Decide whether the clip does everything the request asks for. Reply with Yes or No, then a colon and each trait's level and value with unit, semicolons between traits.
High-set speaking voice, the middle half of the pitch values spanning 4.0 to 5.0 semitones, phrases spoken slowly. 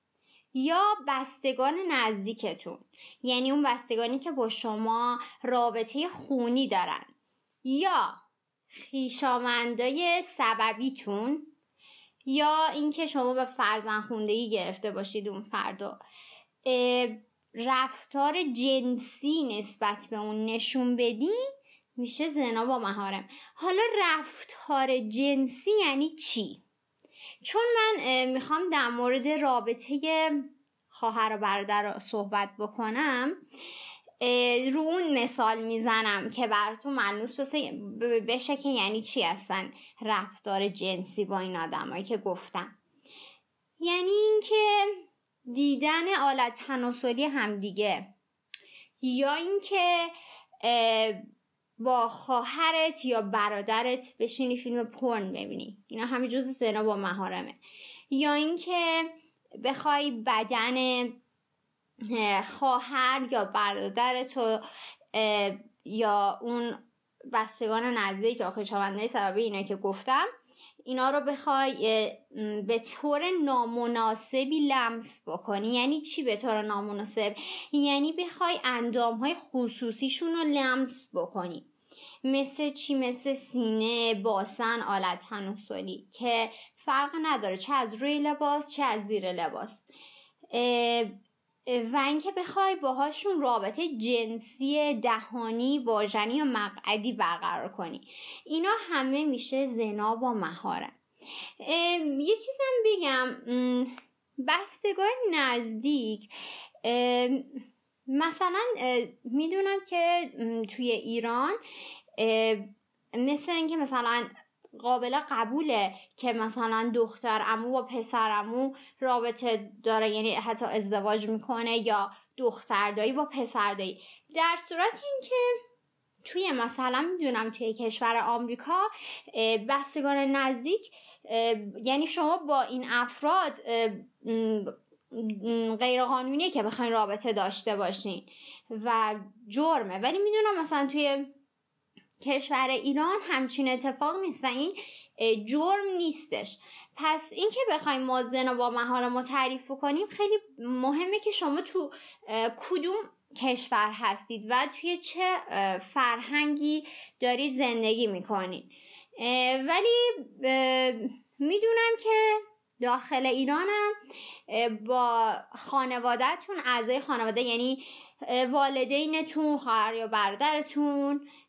Yes: very high, 255 Hz; average, 4.6 semitones; slow, 100 wpm